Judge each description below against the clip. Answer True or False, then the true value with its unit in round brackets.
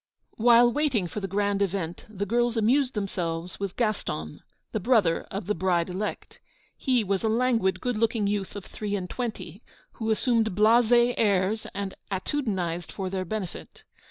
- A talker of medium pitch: False (205 Hz)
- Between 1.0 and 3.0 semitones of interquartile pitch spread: False (3.6 semitones)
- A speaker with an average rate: True (160 wpm)